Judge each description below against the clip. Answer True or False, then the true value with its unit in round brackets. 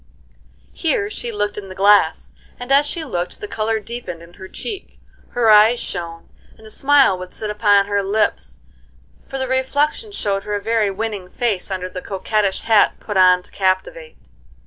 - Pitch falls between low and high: False (210 Hz)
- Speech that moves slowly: False (180 wpm)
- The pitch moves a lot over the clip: False (4.3 semitones)